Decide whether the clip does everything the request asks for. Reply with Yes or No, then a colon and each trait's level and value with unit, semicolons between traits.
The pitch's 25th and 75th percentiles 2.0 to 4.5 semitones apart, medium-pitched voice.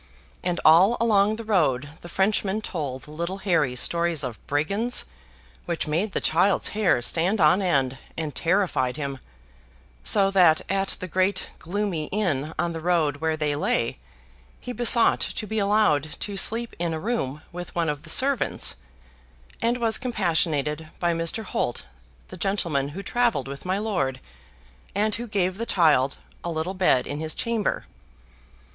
No: average, 5.1 semitones; medium, 175 Hz